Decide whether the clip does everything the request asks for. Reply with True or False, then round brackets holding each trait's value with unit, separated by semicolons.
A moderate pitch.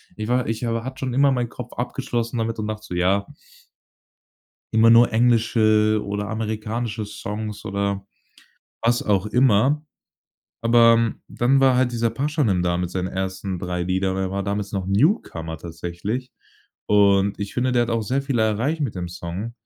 False (110 Hz)